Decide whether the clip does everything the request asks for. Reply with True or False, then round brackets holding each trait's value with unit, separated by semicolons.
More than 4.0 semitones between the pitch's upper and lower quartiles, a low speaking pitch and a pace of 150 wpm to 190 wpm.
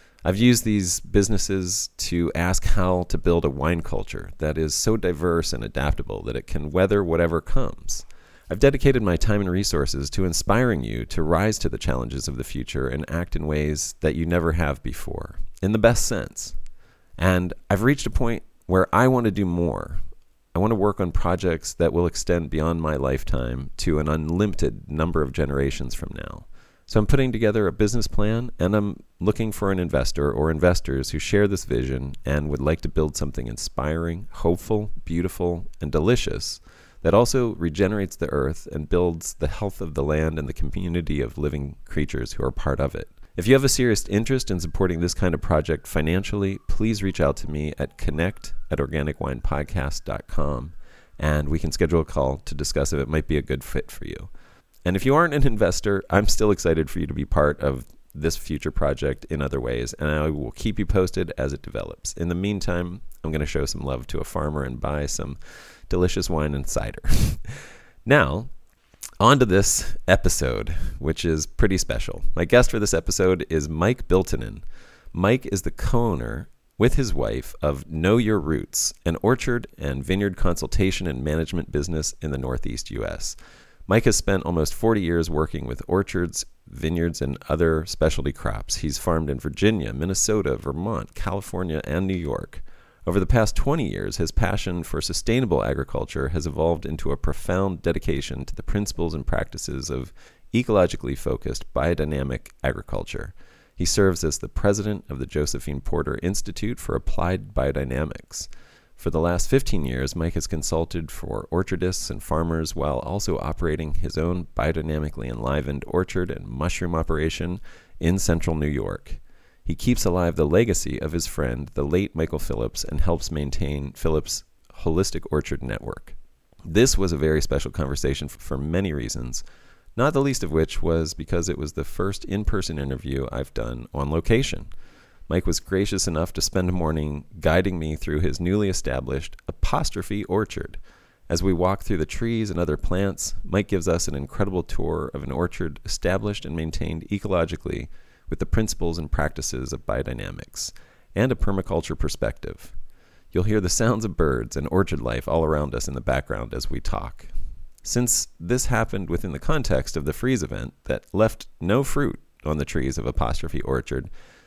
True (4.5 semitones; 85 Hz; 180 wpm)